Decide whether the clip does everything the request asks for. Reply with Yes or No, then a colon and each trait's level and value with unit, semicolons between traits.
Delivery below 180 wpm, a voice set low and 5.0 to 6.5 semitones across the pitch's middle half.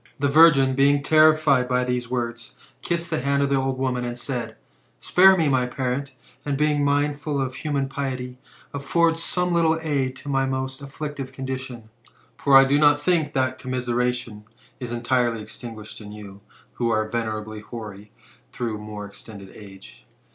No: average, 165 wpm; low, 130 Hz; average, 3.3 semitones